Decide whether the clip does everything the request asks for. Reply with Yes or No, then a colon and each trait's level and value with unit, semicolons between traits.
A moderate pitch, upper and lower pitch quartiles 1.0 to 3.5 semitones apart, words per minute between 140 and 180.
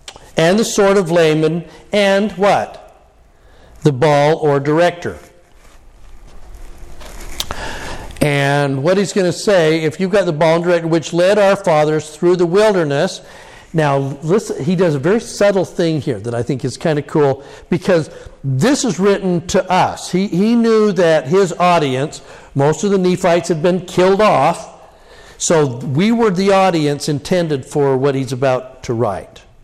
No: medium, 170 Hz; average, 4.9 semitones; average, 160 wpm